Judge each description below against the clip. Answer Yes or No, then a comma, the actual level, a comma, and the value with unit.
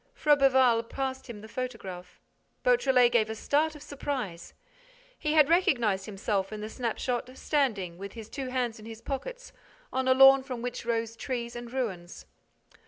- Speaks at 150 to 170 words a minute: Yes, average, 165 wpm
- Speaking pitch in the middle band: No, high, 245 Hz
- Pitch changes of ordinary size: Yes, average, 3.7 semitones